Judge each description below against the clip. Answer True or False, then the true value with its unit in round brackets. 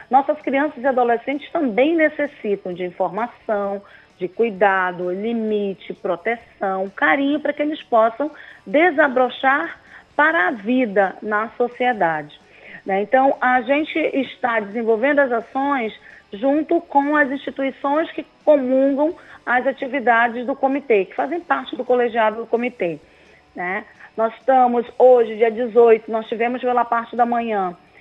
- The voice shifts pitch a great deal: False (4.4 semitones)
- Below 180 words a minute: True (130 wpm)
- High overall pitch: True (245 Hz)